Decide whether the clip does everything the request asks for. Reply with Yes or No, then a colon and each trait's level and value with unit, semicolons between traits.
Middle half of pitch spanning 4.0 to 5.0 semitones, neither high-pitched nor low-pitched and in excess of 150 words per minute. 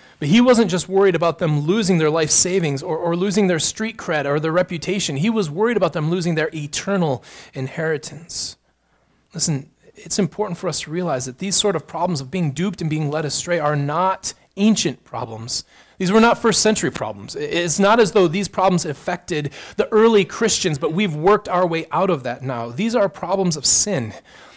Yes: average, 4.4 semitones; medium, 175 Hz; average, 200 wpm